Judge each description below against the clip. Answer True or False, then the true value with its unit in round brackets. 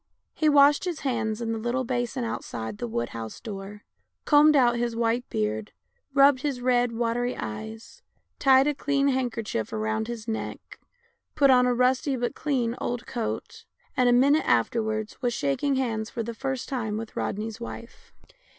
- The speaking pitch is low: False (240 Hz)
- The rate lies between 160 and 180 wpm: True (170 wpm)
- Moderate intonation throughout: True (3.1 semitones)